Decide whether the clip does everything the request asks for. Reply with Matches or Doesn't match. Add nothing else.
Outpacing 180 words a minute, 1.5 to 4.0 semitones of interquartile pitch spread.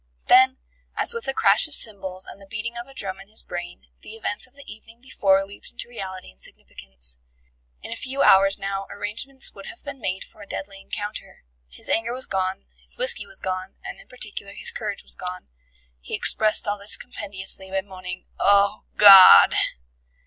Matches